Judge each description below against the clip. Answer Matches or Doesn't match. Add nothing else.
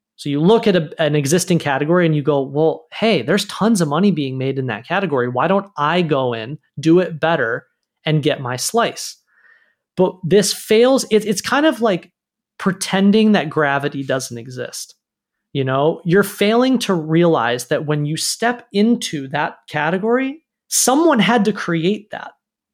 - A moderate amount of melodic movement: Doesn't match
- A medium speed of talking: Matches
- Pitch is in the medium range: Matches